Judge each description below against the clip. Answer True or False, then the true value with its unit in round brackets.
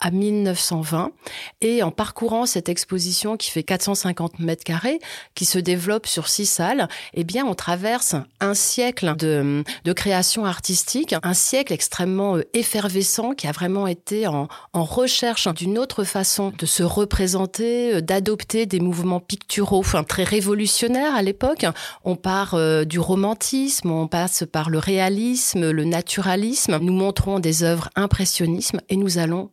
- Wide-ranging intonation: False (3.6 semitones)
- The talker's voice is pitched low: False (190 Hz)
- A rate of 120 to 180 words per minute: True (150 wpm)